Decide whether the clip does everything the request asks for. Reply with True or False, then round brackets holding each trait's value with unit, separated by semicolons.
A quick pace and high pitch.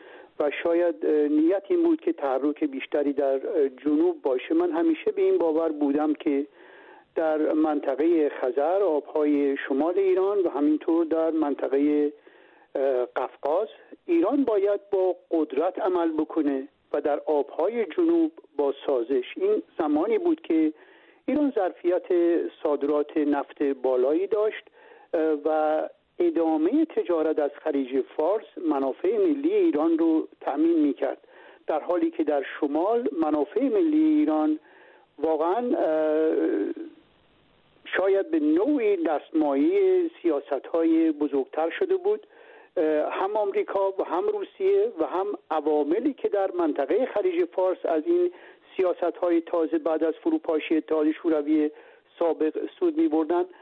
False (120 wpm; 215 Hz)